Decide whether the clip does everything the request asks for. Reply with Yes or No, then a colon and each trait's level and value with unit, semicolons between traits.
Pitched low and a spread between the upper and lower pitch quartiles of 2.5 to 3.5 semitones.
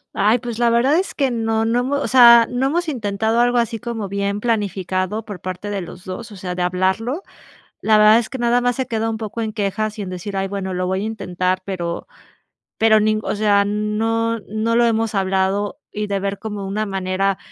No: high, 215 Hz; average, 2.9 semitones